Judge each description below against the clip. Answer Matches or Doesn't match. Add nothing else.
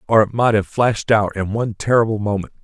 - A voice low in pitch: Matches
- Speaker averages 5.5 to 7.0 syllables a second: Matches